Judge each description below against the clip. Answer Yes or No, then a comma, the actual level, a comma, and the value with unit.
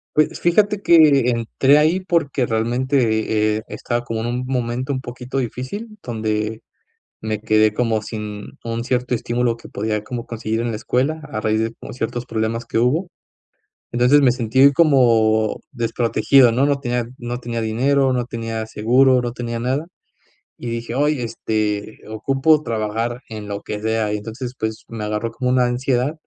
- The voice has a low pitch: Yes, low, 120 Hz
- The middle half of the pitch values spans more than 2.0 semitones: Yes, average, 2.9 semitones